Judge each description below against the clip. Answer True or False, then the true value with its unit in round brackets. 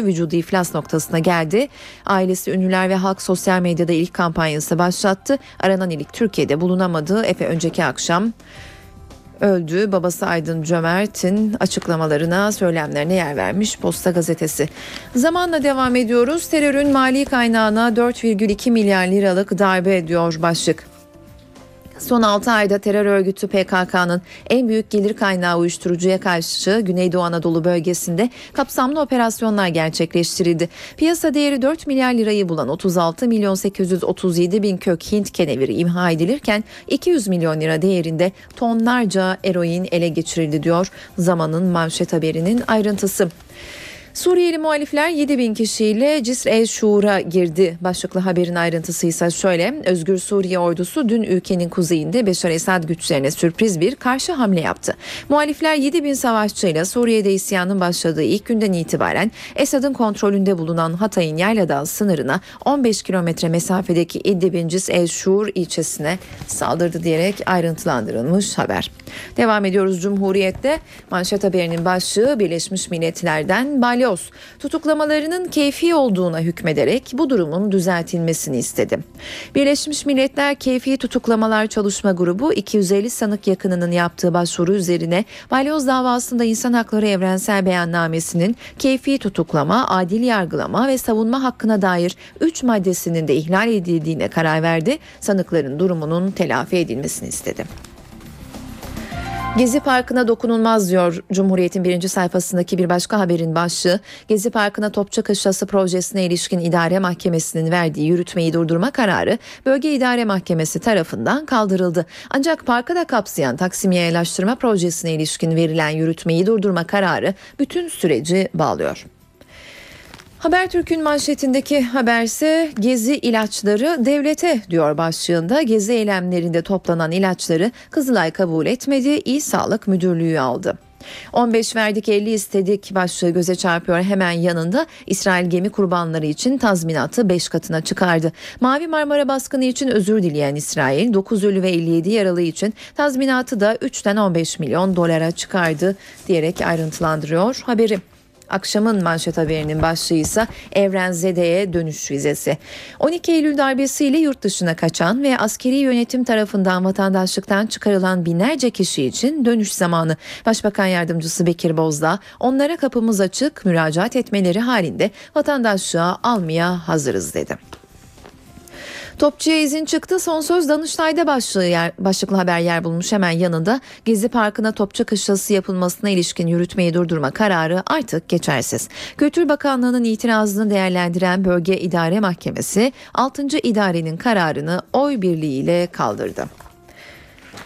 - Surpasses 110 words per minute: True (120 wpm)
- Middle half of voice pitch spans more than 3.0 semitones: True (5.2 semitones)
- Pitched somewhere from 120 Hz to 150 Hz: False (195 Hz)